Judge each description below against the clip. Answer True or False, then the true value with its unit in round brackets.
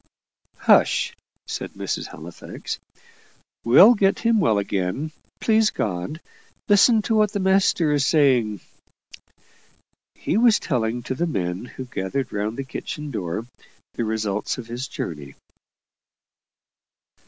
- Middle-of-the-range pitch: False (130 Hz)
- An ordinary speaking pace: False (120 wpm)